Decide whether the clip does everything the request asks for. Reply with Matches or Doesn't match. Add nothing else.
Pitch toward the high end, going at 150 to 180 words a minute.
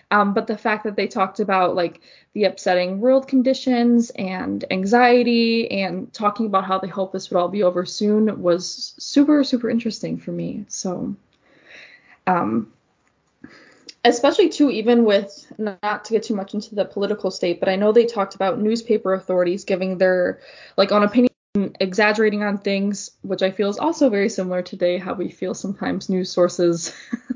Matches